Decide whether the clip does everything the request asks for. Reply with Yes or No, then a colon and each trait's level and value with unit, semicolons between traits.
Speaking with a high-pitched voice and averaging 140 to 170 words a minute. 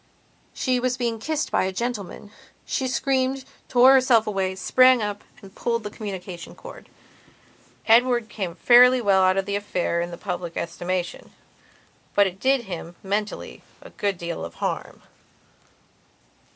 Yes: high, 205 Hz; average, 150 wpm